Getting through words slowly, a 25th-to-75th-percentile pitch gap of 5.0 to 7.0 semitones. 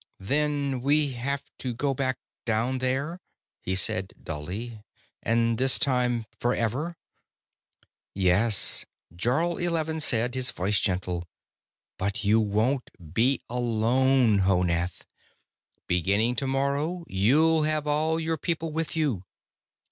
Yes: slow, 110 wpm; wide, 5.5 semitones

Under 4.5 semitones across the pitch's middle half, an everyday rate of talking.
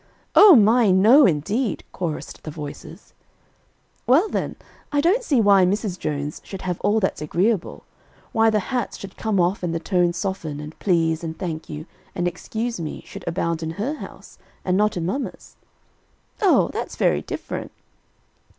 No: average, 5.1 semitones; average, 165 wpm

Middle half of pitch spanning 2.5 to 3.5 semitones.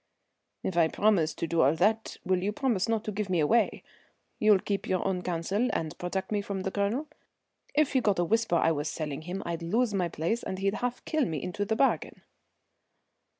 No: average, 4.4 semitones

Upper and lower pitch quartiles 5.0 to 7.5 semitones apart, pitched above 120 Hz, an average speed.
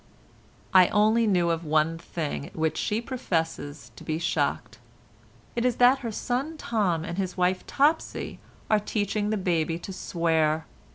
Yes: average, 5.3 semitones; medium, 185 Hz; average, 160 wpm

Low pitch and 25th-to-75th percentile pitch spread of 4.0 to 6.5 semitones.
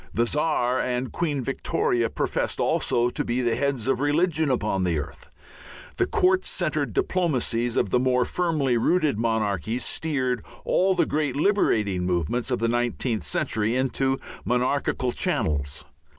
Yes: low, 125 Hz; average, 4.3 semitones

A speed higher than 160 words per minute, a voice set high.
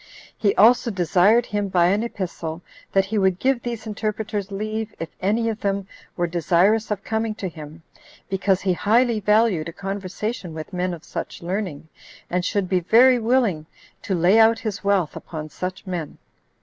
Yes: average, 175 wpm; high, 200 Hz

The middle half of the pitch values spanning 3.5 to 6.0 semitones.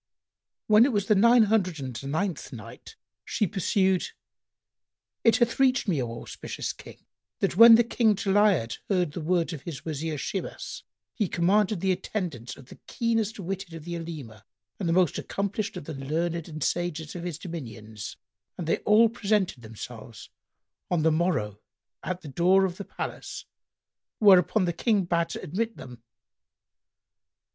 Yes: average, 4.8 semitones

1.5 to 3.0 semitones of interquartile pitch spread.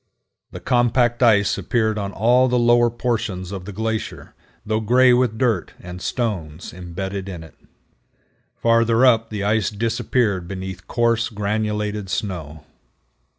No: average, 3.6 semitones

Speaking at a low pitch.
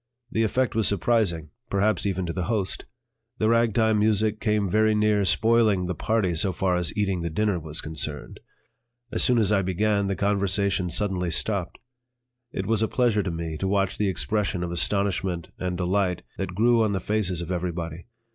Yes: low, 100 Hz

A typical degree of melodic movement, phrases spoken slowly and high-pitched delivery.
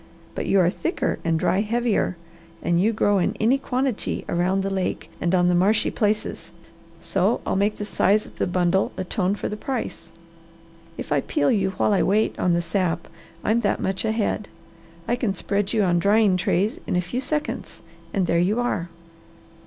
No: average, 3.3 semitones; average, 190 wpm; high, 195 Hz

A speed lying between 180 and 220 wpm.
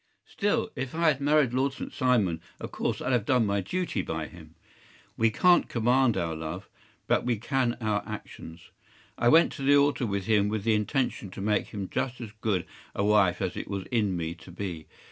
Yes: fast, 205 wpm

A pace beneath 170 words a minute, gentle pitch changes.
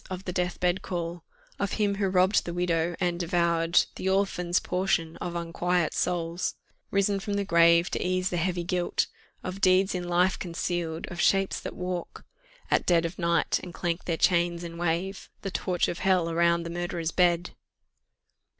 No: average, 175 wpm; narrow, 1.4 semitones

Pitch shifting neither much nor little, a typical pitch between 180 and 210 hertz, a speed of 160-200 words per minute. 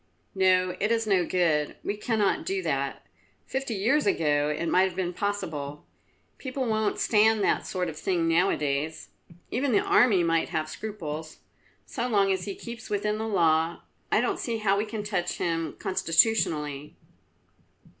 Yes: average, 4.8 semitones; high, 190 Hz; average, 165 wpm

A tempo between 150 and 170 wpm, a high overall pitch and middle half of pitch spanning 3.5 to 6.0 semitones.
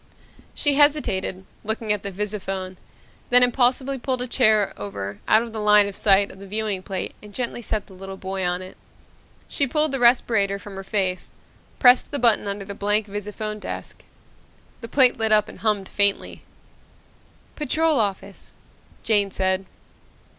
Yes: average, 165 wpm; high, 210 Hz; average, 3.8 semitones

